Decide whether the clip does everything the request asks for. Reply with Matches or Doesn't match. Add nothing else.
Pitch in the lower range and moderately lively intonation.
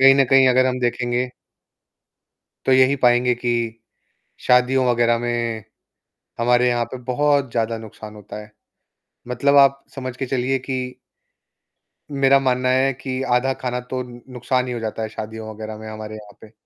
Doesn't match